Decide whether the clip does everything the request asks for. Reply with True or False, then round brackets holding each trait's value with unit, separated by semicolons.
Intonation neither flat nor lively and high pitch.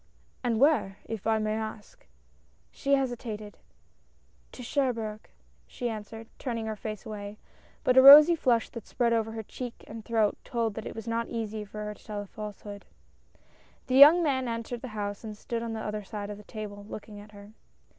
False (2.3 semitones; 220 Hz)